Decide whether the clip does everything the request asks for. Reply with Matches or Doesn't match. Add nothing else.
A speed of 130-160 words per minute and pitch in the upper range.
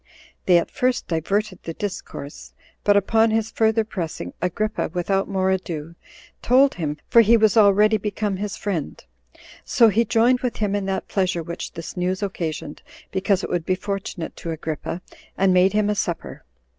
Doesn't match